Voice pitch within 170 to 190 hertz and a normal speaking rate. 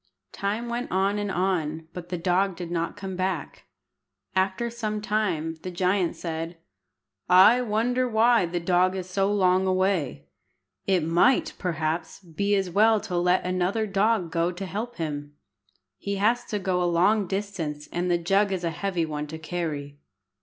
Yes: medium, 185 Hz; average, 165 wpm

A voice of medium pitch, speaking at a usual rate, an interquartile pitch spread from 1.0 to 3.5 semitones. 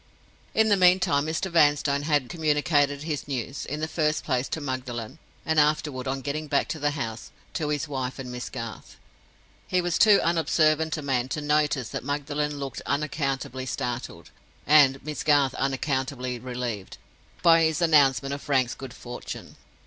Yes: medium, 145 Hz; average, 160 wpm; average, 2.8 semitones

